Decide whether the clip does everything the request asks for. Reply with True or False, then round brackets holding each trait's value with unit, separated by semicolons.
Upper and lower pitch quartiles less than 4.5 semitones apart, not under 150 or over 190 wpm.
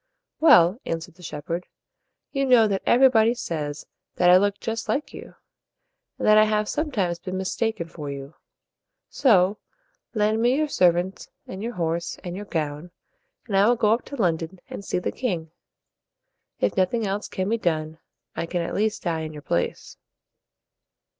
False (4.8 semitones; 180 wpm)